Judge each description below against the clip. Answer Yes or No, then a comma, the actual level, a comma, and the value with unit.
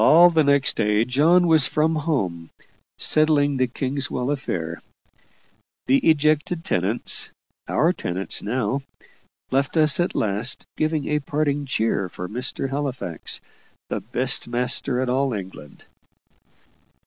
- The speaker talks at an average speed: No, slow, 125 wpm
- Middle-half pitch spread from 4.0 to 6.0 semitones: Yes, average, 5.2 semitones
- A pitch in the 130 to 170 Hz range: Yes, low, 135 Hz